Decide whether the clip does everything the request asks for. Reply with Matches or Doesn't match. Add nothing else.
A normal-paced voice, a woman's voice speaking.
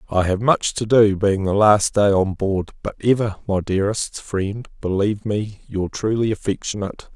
Doesn't match